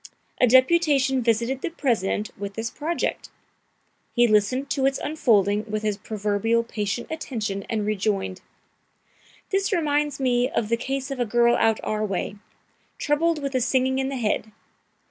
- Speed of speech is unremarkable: Yes, average, 155 wpm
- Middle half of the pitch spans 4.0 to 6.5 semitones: Yes, average, 4.3 semitones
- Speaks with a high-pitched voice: Yes, high, 240 Hz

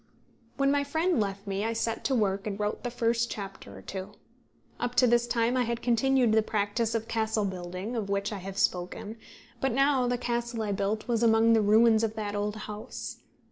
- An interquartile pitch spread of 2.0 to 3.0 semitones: Yes, average, 2.7 semitones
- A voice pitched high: Yes, high, 225 Hz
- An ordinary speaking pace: No, fast, 210 wpm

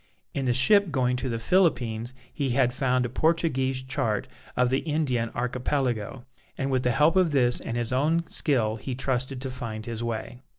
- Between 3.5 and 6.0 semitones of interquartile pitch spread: No, narrow, 2.5 semitones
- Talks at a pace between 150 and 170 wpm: No, average, 185 wpm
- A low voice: Yes, low, 130 Hz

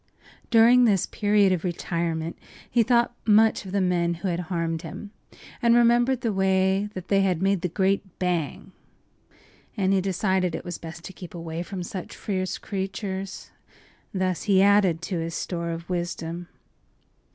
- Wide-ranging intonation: No, average, 2.8 semitones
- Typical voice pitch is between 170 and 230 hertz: Yes, high, 190 Hz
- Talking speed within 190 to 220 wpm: No, average, 160 wpm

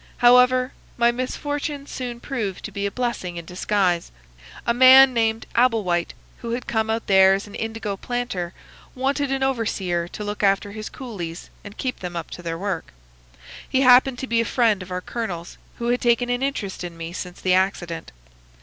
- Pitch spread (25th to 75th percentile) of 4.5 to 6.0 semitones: Yes, average, 5.0 semitones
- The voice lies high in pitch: Yes, high, 220 Hz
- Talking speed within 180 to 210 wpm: Yes, average, 190 wpm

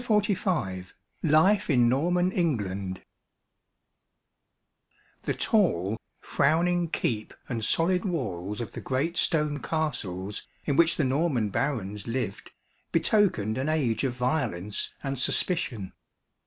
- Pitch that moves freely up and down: Yes, wide, 7.6 semitones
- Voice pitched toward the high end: No, low, 135 Hz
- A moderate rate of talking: No, slow, 110 wpm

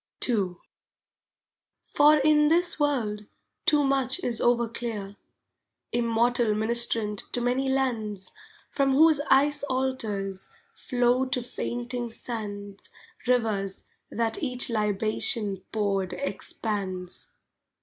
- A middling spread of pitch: Yes, average, 4.0 semitones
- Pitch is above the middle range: Yes, high, 235 Hz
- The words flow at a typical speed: No, slow, 95 wpm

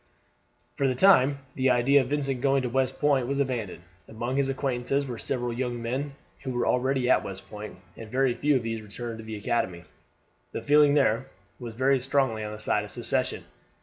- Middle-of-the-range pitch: No, low, 125 Hz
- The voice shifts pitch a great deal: No, average, 3.0 semitones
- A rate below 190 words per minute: No, average, 200 wpm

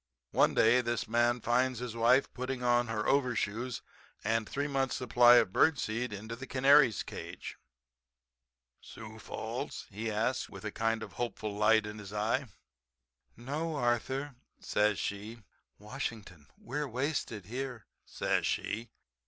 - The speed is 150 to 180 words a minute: No, average, 140 wpm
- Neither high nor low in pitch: No, low, 120 Hz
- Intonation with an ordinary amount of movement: Yes, average, 3.0 semitones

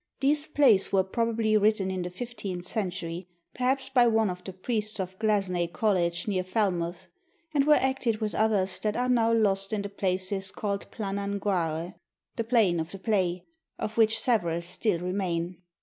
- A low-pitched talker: No, high, 200 Hz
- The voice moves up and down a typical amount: Yes, average, 3.5 semitones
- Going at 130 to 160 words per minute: No, average, 170 wpm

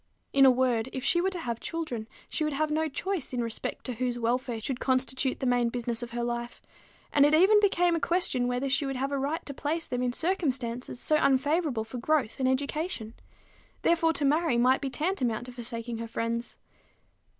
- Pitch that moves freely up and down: No, average, 4.4 semitones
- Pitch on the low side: No, very high, 260 Hz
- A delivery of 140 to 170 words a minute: No, fast, 205 wpm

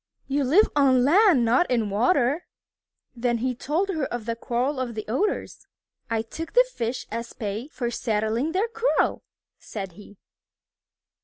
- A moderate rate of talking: Yes, average, 160 wpm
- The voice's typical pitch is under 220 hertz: No, very high, 250 Hz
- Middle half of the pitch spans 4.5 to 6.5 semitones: Yes, average, 5.2 semitones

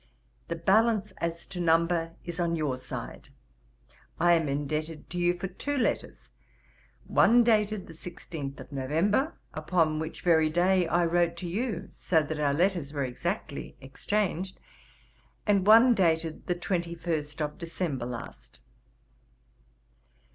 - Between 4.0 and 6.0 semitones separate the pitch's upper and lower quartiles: No, average, 3.2 semitones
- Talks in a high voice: No, medium, 170 Hz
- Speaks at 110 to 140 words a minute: Yes, slow, 135 wpm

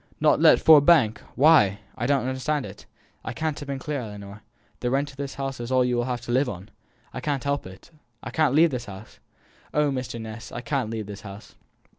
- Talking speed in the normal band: No, fast, 225 wpm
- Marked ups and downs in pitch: No, average, 4.2 semitones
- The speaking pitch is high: No, low, 130 Hz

